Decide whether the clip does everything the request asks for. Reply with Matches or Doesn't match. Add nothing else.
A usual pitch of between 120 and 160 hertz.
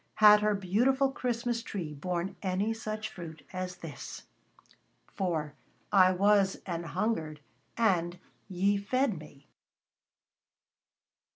Doesn't match